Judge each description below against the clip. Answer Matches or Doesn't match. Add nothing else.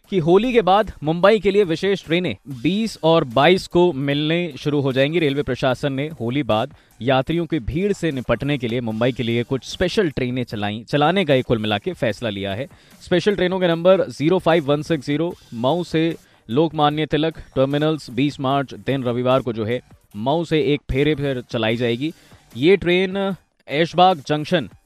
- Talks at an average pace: Matches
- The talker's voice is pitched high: Doesn't match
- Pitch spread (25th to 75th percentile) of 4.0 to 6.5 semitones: Matches